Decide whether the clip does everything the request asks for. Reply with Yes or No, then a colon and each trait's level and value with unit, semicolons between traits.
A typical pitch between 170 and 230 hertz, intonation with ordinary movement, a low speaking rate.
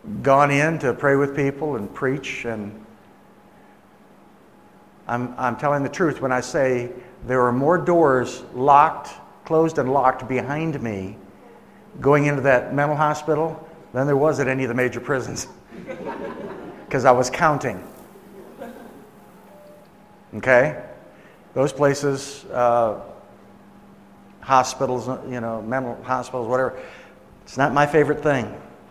No: low, 135 Hz; average, 3.1 semitones; slow, 125 wpm